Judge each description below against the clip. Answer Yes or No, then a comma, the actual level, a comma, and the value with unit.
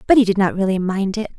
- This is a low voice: No, high, 200 Hz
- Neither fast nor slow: No, fast, 305 wpm